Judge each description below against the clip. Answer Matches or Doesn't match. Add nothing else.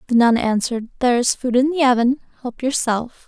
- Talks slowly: Doesn't match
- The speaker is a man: Doesn't match